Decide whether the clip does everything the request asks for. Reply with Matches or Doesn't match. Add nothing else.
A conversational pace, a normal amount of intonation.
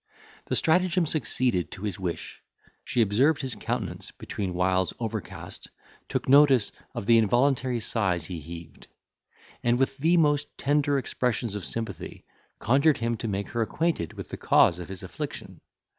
Doesn't match